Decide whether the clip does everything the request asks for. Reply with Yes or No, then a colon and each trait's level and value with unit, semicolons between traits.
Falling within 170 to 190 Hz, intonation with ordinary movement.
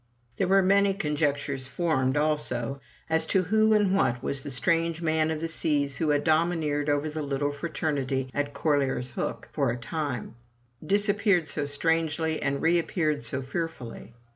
No: medium, 150 Hz; average, 3.0 semitones